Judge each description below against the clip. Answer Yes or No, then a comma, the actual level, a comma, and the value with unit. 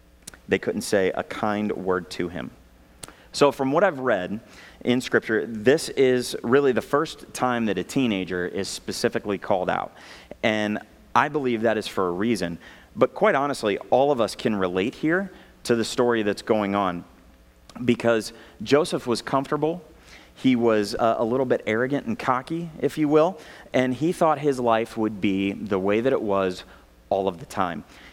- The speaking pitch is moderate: No, low, 115 Hz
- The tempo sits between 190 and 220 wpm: No, average, 175 wpm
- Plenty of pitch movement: Yes, wide, 6.2 semitones